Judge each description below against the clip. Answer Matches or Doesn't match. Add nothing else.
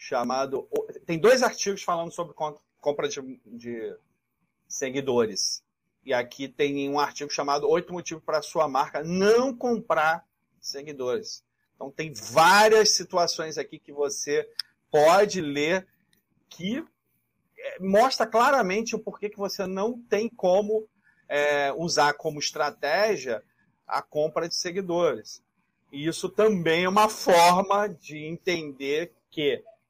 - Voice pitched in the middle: Matches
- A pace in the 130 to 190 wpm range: Doesn't match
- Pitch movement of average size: Doesn't match